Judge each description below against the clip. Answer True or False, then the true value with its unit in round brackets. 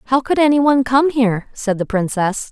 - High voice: True (245 Hz)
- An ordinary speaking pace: False (215 wpm)